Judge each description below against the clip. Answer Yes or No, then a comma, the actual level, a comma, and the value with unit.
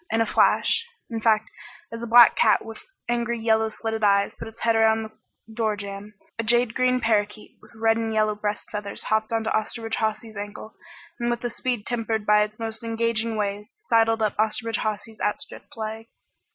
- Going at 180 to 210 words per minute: Yes, average, 190 wpm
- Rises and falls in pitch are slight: Yes, narrow, 1.2 semitones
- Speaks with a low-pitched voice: No, high, 220 Hz